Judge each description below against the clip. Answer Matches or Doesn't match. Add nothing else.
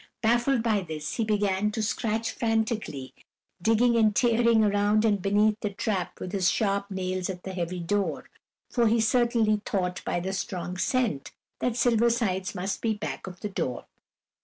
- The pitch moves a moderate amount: Matches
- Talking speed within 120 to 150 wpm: Doesn't match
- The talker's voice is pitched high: Matches